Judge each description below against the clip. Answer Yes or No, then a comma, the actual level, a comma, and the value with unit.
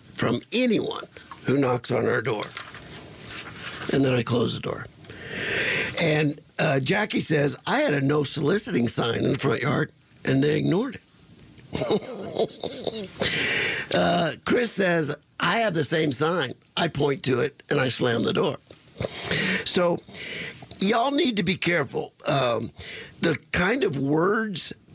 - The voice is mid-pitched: Yes, medium, 155 Hz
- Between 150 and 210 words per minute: No, average, 140 wpm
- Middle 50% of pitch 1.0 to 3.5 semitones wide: No, average, 4.7 semitones